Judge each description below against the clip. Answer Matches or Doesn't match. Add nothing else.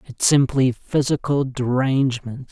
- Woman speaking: Doesn't match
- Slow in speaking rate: Matches